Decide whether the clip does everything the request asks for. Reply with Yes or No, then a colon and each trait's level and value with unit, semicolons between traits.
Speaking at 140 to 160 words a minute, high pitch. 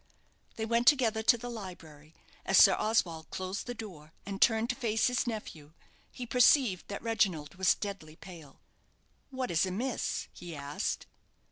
Yes: average, 155 wpm; high, 205 Hz